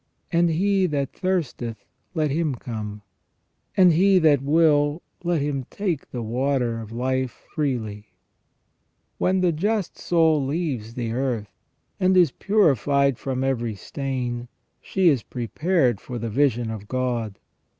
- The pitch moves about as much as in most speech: No, wide, 5.7 semitones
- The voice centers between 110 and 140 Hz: Yes, low, 135 Hz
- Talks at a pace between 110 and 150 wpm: Yes, slow, 135 wpm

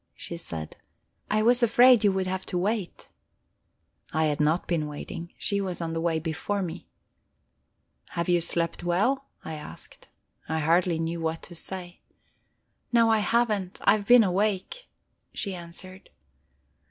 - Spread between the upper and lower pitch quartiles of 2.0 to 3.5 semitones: No, average, 3.9 semitones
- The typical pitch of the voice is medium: Yes, medium, 180 Hz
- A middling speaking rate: Yes, average, 155 wpm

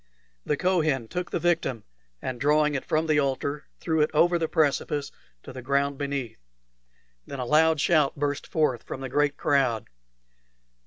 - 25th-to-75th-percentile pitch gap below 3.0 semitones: Yes, narrow, 2.5 semitones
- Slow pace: No, average, 165 wpm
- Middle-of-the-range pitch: Yes, medium, 145 Hz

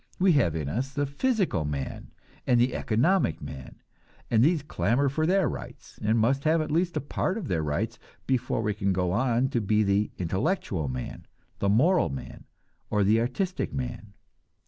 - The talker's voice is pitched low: Yes, low, 120 Hz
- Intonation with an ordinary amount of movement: No, wide, 7.5 semitones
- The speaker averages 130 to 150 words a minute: No, average, 180 wpm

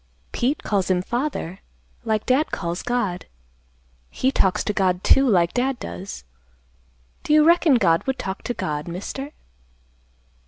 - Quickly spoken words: No, average, 145 wpm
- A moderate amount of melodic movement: No, wide, 6.6 semitones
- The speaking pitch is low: No, high, 215 Hz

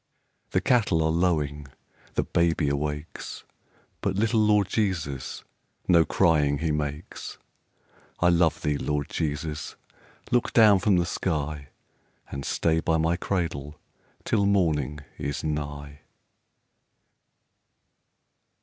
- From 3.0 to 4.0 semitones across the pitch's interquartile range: Yes, average, 3.7 semitones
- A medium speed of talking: No, slow, 110 wpm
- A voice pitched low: Yes, very low, 80 Hz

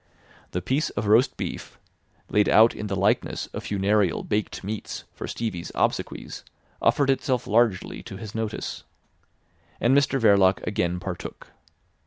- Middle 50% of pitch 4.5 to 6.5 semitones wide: No, average, 3.1 semitones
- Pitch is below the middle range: Yes, low, 105 Hz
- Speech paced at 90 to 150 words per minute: Yes, average, 140 wpm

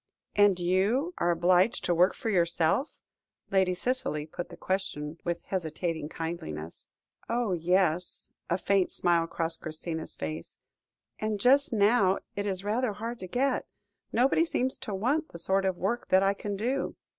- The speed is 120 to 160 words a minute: Yes, average, 155 wpm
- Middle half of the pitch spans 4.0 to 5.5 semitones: Yes, average, 4.5 semitones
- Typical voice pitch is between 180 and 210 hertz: Yes, high, 190 Hz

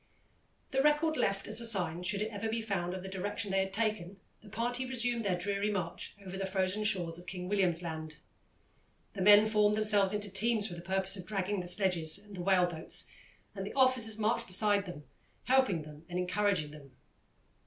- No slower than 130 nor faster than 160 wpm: No, average, 195 wpm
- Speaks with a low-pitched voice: No, high, 195 Hz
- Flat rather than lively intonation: No, average, 3.0 semitones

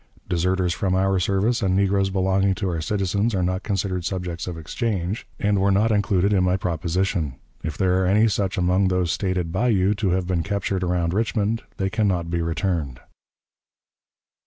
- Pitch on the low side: Yes, very low, 95 Hz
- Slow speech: No, average, 185 wpm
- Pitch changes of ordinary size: No, narrow, 2.0 semitones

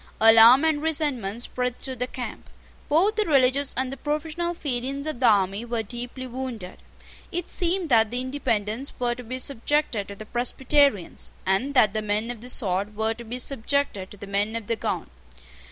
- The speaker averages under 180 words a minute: No, average, 185 wpm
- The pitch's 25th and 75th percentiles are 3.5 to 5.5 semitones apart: Yes, average, 4.3 semitones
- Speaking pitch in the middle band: No, high, 245 Hz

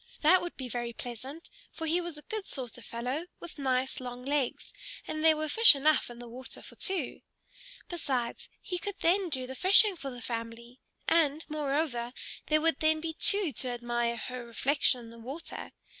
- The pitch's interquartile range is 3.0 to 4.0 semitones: No, average, 4.9 semitones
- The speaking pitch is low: No, very high, 275 Hz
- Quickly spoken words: No, average, 190 wpm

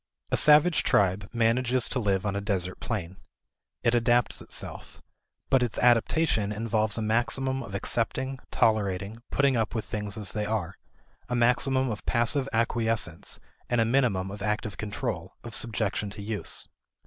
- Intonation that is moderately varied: Yes, average, 3.1 semitones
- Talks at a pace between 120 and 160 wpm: Yes, average, 155 wpm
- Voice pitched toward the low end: Yes, low, 110 Hz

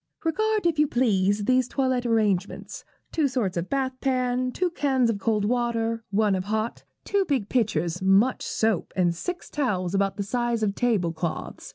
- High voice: Yes, high, 230 Hz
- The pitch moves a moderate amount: Yes, average, 4.6 semitones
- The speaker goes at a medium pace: Yes, average, 175 wpm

